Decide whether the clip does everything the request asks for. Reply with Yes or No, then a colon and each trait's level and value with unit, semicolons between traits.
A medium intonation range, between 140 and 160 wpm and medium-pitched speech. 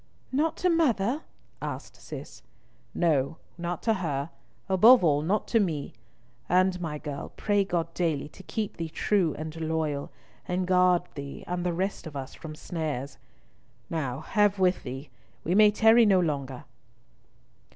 Yes: average, 4.4 semitones; average, 150 wpm; medium, 175 Hz